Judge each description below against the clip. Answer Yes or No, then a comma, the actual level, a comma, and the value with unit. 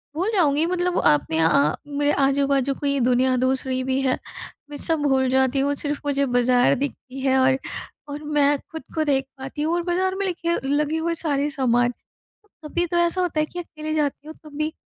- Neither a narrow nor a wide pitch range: Yes, average, 3.1 semitones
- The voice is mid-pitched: No, very high, 285 Hz